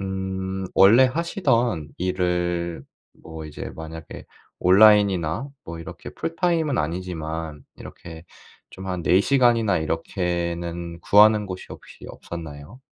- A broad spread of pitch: No, average, 4.1 semitones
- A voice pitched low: Yes, very low, 90 Hz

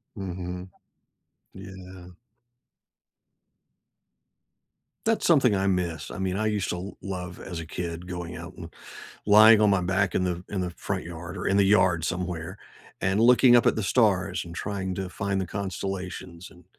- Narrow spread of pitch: Yes, narrow, 2.0 semitones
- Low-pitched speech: Yes, very low, 95 Hz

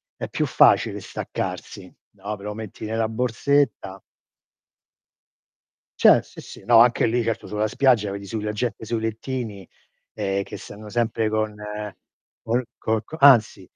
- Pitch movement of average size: No, narrow, 2.2 semitones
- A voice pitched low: Yes, low, 110 Hz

